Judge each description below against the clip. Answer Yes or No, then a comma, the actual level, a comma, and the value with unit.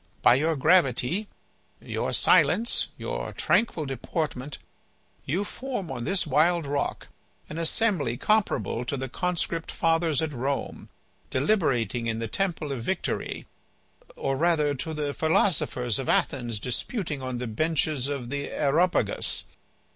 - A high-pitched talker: No, medium, 150 Hz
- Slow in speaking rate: Yes, slow, 130 wpm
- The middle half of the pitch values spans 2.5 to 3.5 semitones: No, average, 4.7 semitones